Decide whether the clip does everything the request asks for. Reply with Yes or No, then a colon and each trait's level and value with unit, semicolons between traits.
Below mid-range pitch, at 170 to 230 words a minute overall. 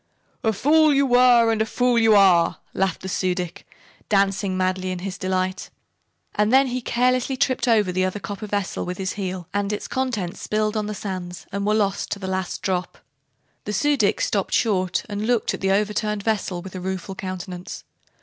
No: high, 200 Hz; average, 200 wpm